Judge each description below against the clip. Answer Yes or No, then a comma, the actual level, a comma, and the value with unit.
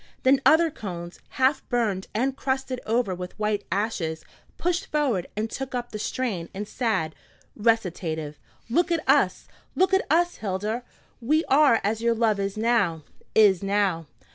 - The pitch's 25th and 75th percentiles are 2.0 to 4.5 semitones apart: No, wide, 5.4 semitones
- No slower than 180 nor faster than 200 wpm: No, average, 155 wpm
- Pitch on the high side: Yes, high, 225 Hz